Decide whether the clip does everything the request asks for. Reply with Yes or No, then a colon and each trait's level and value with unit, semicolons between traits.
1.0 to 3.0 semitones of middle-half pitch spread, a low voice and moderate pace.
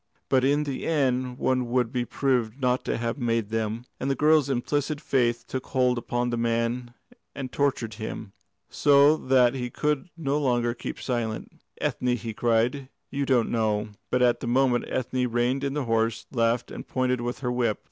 Yes: narrow, 2.4 semitones; low, 125 Hz; average, 190 wpm